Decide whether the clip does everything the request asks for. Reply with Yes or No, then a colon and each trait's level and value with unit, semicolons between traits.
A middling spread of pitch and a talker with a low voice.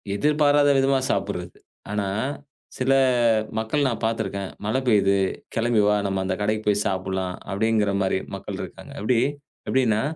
Yes: average, 4.1 semitones; low, 110 Hz